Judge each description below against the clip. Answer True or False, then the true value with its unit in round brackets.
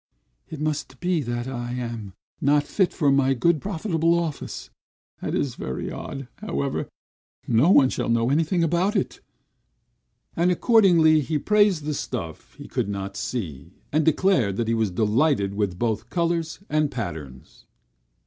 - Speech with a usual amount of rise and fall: False (6.4 semitones)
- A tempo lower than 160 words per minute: True (150 wpm)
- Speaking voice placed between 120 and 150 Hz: True (140 Hz)